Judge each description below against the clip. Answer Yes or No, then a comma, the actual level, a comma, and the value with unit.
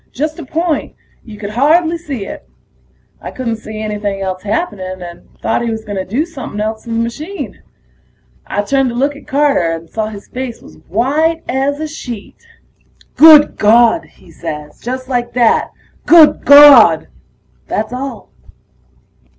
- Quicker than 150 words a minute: Yes, average, 160 wpm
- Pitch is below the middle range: No, high, 240 Hz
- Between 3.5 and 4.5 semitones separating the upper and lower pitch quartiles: No, wide, 5.6 semitones